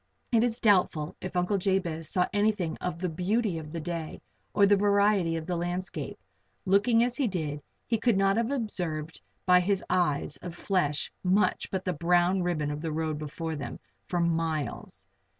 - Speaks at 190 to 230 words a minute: No, average, 175 wpm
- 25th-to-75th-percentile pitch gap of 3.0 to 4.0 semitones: Yes, average, 3.7 semitones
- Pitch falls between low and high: Yes, medium, 180 Hz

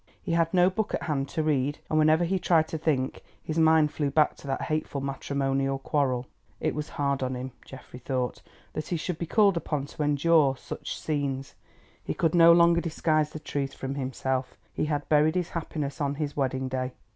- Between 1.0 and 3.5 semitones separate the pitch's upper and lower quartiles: Yes, average, 3.0 semitones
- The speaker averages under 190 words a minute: No, average, 200 wpm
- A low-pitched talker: No, medium, 150 Hz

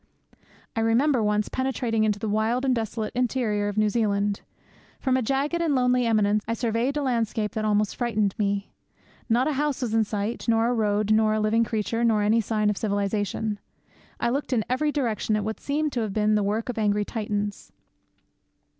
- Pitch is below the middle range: No, high, 220 Hz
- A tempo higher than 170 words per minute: Yes, average, 195 wpm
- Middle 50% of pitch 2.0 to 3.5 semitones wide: Yes, average, 2.9 semitones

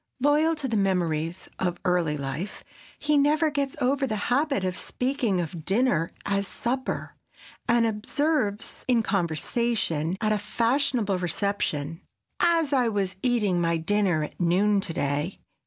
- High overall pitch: Yes, high, 205 Hz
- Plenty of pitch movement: Yes, wide, 6.6 semitones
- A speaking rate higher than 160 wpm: No, average, 140 wpm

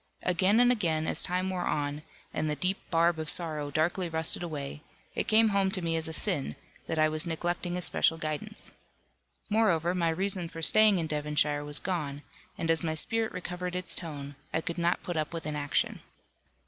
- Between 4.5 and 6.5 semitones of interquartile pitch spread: No, average, 3.0 semitones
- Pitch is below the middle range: No, medium, 165 Hz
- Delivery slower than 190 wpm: No, average, 195 wpm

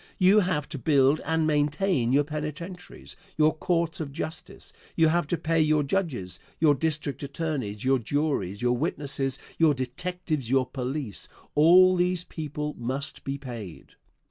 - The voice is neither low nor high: Yes, medium, 150 Hz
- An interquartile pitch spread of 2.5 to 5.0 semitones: Yes, average, 3.5 semitones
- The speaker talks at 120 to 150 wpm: Yes, average, 145 wpm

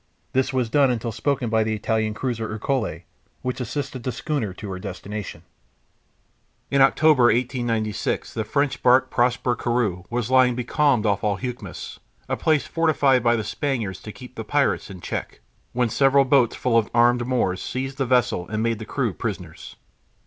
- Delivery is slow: No, average, 170 wpm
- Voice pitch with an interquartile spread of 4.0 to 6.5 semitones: No, average, 3.3 semitones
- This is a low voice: Yes, low, 120 Hz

